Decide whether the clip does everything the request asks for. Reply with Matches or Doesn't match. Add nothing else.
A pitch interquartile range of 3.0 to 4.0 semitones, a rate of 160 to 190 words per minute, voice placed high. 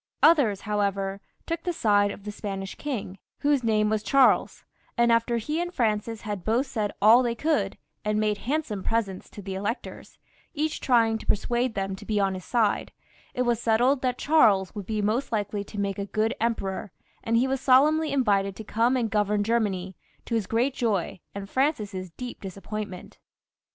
Matches